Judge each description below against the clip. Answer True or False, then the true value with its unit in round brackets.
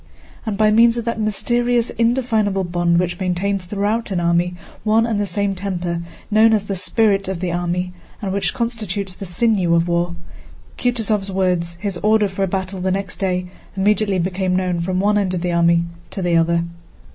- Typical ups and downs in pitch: True (3.2 semitones)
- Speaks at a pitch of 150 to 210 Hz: True (190 Hz)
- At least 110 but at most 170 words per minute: False (185 wpm)